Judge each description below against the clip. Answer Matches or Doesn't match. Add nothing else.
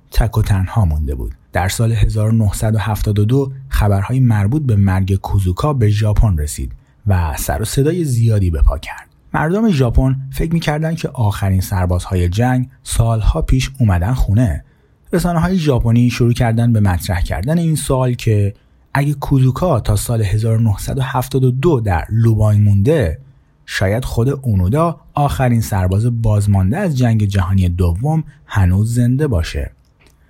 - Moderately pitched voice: Doesn't match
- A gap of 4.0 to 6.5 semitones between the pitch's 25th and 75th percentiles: Matches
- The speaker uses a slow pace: Doesn't match